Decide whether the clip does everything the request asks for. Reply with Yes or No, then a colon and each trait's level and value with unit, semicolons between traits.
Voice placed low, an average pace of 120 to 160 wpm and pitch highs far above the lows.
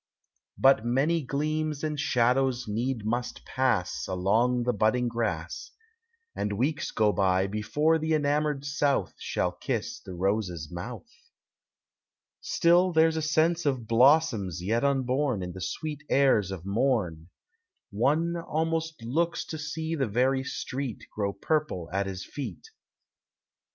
Yes: low, 130 Hz; slow, 135 wpm; wide, 6.5 semitones